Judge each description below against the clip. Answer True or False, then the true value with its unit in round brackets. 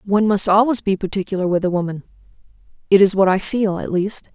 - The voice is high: True (195 Hz)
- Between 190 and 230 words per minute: True (205 wpm)